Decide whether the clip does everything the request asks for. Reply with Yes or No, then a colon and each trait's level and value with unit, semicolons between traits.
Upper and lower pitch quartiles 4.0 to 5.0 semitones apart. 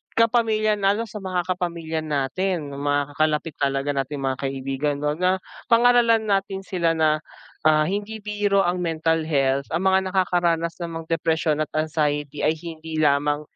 Yes: average, 4.4 semitones